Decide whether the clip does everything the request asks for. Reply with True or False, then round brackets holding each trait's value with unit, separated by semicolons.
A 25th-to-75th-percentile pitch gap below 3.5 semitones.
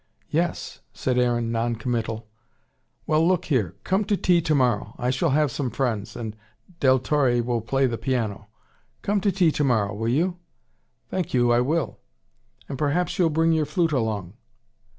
False (5.2 semitones)